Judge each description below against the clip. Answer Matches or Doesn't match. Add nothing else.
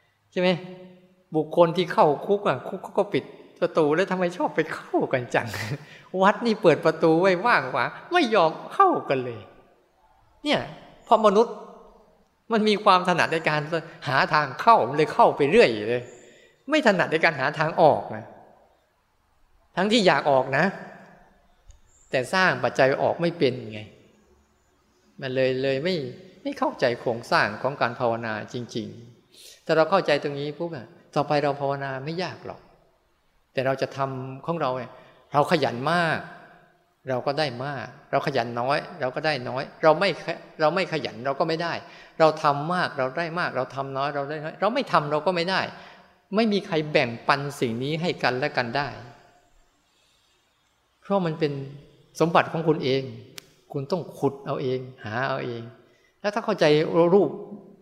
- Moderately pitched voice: Matches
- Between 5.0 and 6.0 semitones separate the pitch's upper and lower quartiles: Matches